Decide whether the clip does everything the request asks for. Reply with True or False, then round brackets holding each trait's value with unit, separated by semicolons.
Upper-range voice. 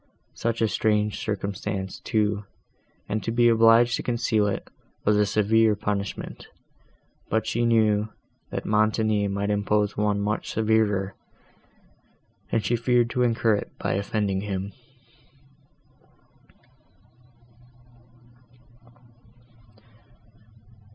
False (105 Hz)